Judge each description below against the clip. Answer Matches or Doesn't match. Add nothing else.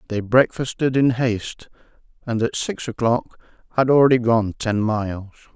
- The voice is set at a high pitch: Doesn't match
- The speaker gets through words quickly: Doesn't match